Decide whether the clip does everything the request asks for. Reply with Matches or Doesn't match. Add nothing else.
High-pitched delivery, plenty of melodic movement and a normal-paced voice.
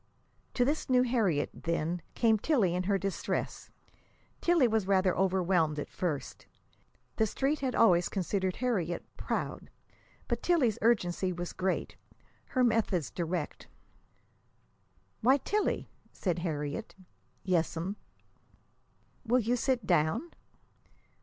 Doesn't match